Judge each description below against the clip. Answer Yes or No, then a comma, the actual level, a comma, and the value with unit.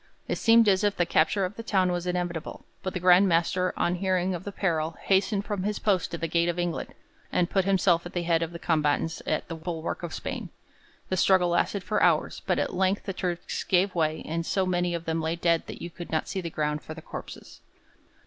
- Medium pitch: Yes, medium, 175 Hz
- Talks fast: Yes, fast, 235 wpm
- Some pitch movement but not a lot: No, narrow, 2.2 semitones